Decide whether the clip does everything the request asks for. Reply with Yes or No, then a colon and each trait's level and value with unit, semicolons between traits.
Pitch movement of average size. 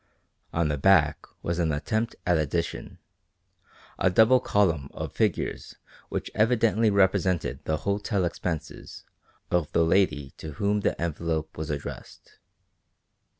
Yes: average, 4.3 semitones